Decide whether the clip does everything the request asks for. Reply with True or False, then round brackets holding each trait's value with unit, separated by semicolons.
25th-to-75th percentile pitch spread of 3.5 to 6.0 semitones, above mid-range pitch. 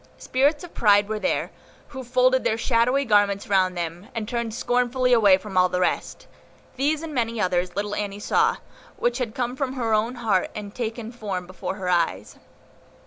True (4.1 semitones; 220 Hz)